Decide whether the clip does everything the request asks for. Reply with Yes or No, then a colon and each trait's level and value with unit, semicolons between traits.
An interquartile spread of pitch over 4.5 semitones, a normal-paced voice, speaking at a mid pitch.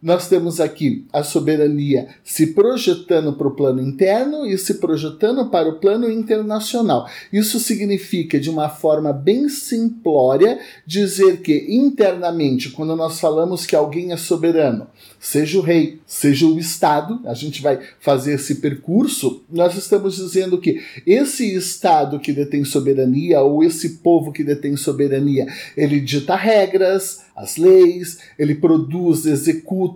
Yes: average, 4.9 semitones; average, 140 wpm; medium, 165 Hz